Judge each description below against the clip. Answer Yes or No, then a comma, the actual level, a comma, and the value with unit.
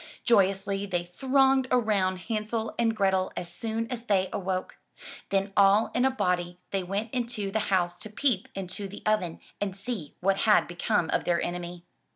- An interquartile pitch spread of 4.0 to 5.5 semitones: No, average, 3.3 semitones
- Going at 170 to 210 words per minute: Yes, average, 175 wpm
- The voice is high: Yes, high, 195 Hz